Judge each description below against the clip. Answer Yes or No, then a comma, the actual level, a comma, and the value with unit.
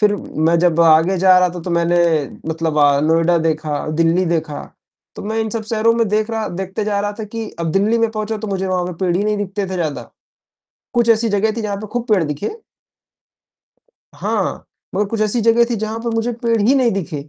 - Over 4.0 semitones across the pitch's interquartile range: Yes, average, 4.5 semitones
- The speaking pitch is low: No, high, 200 Hz